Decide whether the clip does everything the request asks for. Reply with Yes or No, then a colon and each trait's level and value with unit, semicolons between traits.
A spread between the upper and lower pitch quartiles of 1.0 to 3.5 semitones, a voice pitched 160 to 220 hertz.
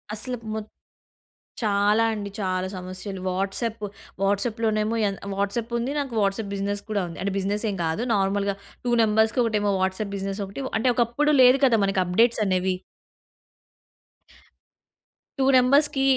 Yes: average, 2.8 semitones; high, 205 Hz